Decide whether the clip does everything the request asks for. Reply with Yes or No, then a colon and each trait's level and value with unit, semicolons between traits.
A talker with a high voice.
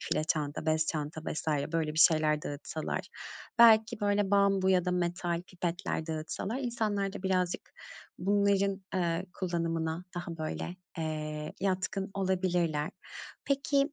No: medium, 180 Hz